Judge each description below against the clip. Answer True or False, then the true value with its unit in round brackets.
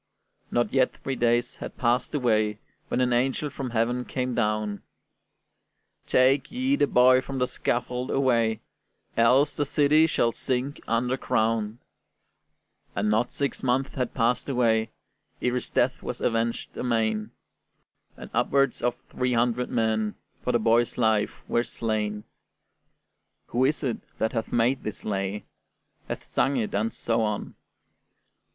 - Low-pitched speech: True (120 Hz)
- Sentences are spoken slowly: False (145 wpm)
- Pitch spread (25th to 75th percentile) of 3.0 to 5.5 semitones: False (2.5 semitones)